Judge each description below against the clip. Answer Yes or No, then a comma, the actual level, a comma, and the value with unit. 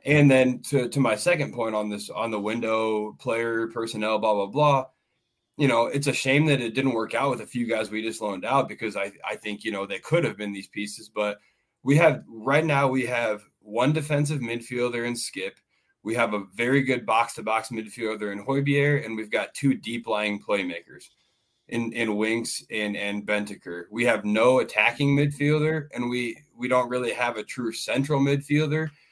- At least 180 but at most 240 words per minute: Yes, average, 200 wpm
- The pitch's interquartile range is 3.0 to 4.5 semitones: Yes, average, 4.1 semitones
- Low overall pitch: Yes, low, 120 Hz